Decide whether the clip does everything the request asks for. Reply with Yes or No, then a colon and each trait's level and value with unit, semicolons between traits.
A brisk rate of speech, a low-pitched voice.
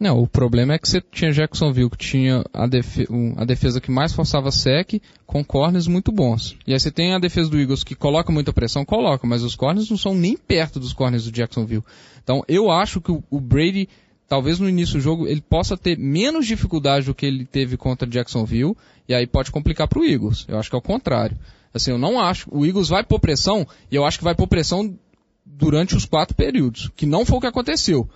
No: fast, 225 wpm; medium, 145 Hz